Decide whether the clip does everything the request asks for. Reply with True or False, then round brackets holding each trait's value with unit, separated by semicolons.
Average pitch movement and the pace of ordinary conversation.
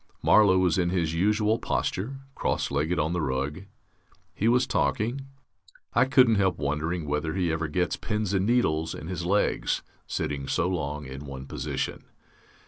False (5.9 semitones; 160 wpm)